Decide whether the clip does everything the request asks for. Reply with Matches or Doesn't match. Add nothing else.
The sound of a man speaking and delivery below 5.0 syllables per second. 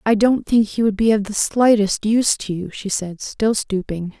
Doesn't match